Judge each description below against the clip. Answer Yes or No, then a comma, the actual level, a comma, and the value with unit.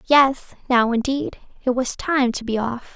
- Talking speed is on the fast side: No, average, 185 wpm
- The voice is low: No, very high, 250 Hz